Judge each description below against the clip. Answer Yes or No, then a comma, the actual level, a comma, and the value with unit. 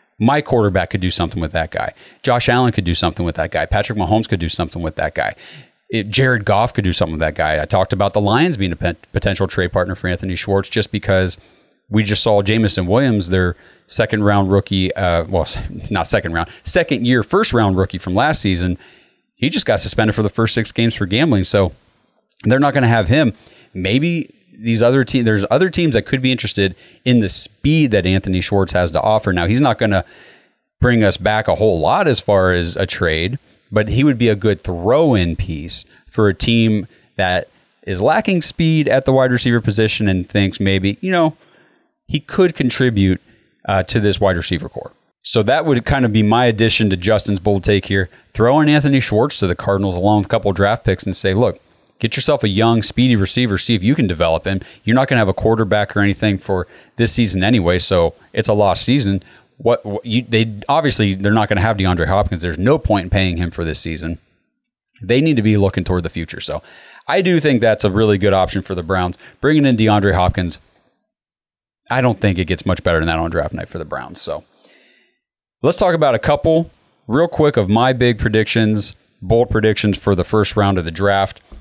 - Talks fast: Yes, fast, 220 wpm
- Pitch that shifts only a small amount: No, average, 4.0 semitones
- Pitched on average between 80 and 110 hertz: Yes, low, 105 Hz